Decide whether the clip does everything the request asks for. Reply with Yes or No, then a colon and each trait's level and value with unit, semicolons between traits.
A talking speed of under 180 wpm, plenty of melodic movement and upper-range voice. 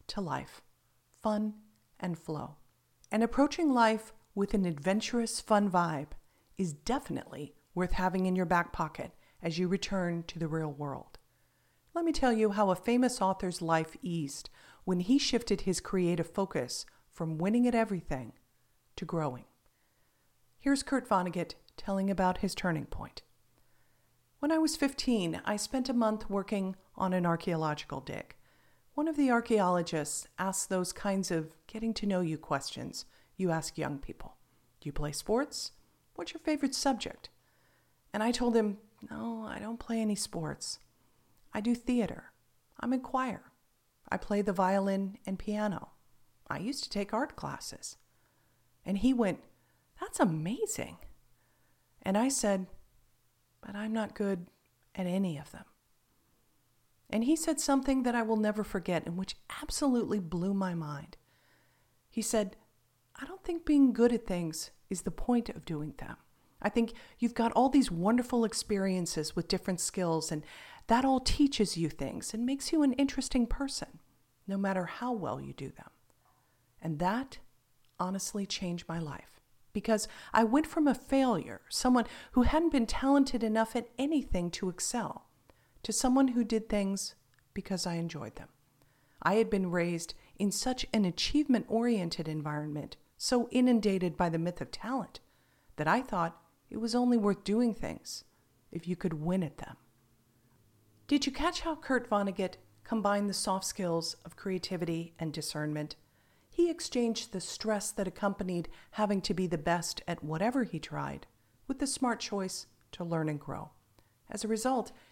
Yes: average, 160 wpm; wide, 5.9 semitones; high, 200 Hz